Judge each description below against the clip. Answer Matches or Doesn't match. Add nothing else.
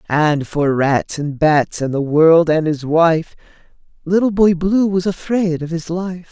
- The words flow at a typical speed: Matches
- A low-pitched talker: Doesn't match